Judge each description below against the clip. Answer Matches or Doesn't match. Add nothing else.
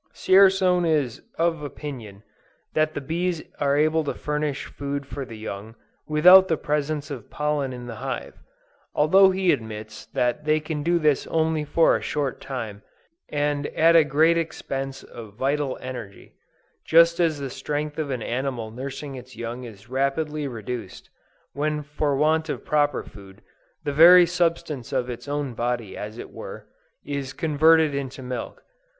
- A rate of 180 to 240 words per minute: Doesn't match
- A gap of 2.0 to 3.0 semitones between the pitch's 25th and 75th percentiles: Doesn't match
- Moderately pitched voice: Matches